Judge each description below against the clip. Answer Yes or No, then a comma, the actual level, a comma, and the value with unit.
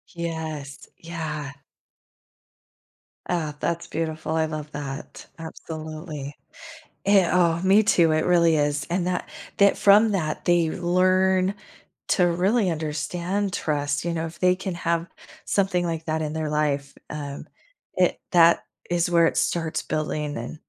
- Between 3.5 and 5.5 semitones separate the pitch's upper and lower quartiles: No, narrow, 2.6 semitones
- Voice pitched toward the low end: No, medium, 165 Hz